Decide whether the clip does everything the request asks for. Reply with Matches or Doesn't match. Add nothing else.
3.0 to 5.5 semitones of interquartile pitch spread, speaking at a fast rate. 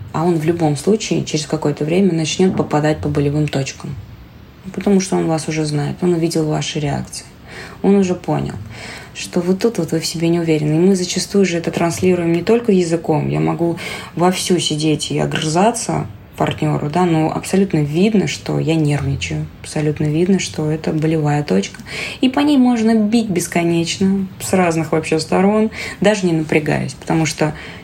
Matches